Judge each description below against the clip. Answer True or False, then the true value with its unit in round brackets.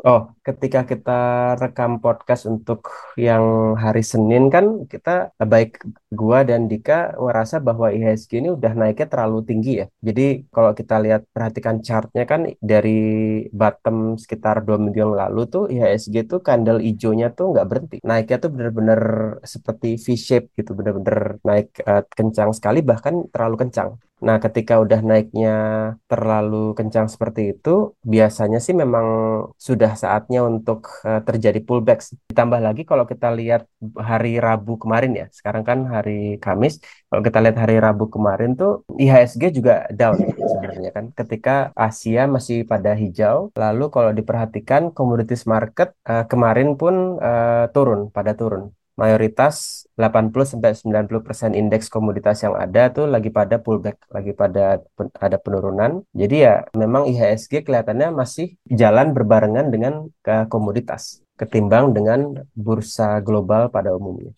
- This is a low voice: True (115 Hz)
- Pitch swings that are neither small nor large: False (2.1 semitones)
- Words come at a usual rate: False (145 wpm)